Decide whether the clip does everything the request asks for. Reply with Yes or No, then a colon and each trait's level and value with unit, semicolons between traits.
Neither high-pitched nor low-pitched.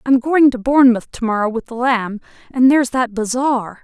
No: high, 245 Hz